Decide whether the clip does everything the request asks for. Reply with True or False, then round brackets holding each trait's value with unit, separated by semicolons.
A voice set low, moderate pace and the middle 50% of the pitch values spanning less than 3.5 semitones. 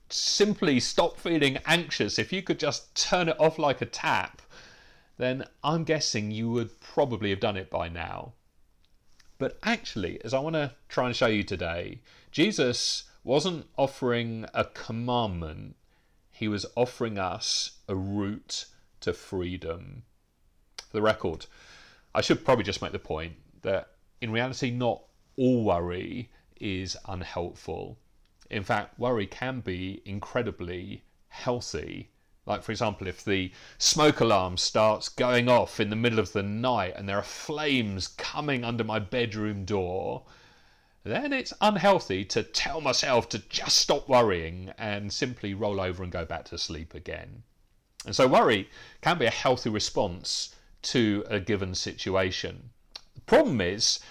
False (110 Hz; 150 wpm; 5.0 semitones)